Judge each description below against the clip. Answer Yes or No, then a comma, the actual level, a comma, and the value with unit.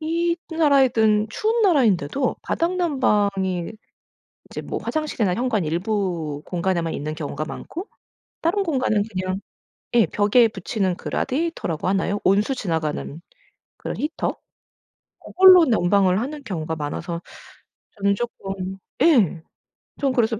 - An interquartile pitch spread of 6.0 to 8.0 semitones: Yes, wide, 7.7 semitones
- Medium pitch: No, high, 210 Hz